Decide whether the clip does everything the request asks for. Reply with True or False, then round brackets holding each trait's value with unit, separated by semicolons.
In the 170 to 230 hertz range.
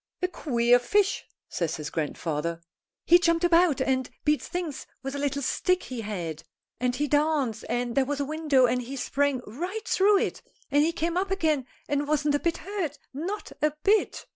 False (290 Hz)